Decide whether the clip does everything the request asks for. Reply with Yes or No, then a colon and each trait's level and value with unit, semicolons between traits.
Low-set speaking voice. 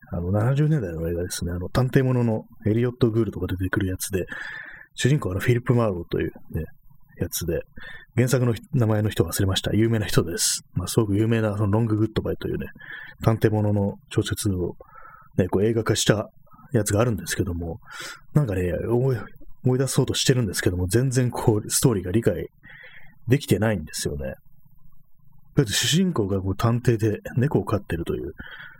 Yes: low, 115 Hz